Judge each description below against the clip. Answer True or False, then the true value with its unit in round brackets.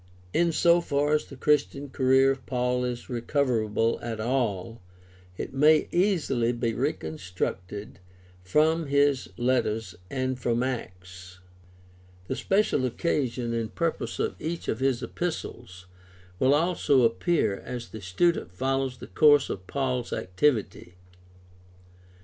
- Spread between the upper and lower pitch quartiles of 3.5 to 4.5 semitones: True (4.2 semitones)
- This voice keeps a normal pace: False (130 wpm)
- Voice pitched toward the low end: True (125 Hz)